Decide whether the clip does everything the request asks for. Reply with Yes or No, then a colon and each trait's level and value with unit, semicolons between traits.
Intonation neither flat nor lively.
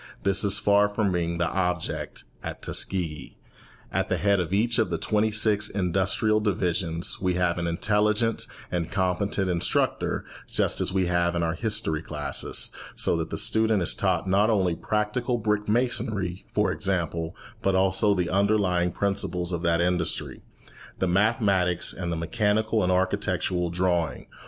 Yes: average, 3.1 semitones